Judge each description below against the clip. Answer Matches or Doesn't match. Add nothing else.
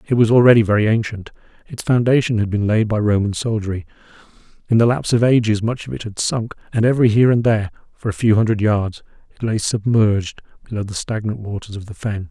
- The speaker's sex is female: Doesn't match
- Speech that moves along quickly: Matches